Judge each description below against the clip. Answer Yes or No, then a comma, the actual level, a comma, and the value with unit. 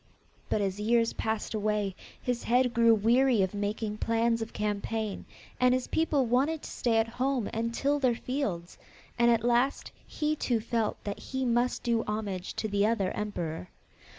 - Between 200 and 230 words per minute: No, average, 175 wpm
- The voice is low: No, high, 230 Hz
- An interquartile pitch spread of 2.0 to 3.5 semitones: Yes, average, 2.9 semitones